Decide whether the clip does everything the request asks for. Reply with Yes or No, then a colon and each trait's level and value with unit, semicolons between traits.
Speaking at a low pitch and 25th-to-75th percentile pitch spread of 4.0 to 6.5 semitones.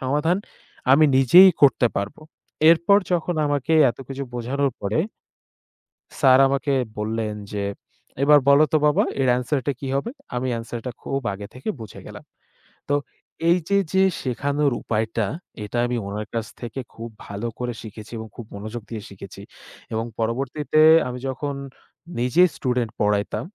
Yes: low, 125 Hz; average, 4.3 semitones